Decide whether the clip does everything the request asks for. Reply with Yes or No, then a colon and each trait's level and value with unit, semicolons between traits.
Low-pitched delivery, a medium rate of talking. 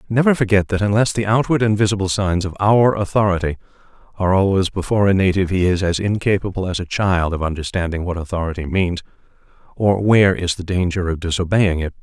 Yes: very low, 95 Hz; average, 185 wpm